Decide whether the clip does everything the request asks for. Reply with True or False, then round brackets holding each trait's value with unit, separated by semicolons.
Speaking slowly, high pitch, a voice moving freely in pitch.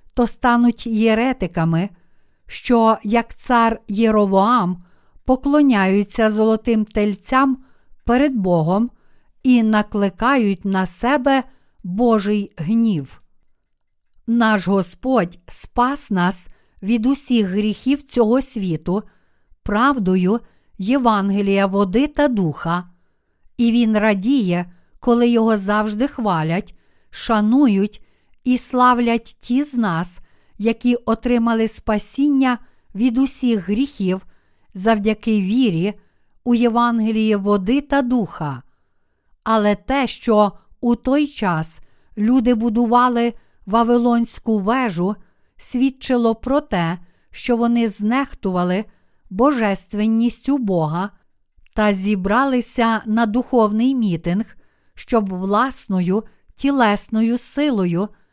False (85 wpm; 225 Hz; 3.7 semitones)